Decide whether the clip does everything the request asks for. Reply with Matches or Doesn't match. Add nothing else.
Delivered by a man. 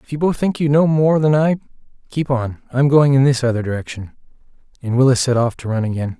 Matches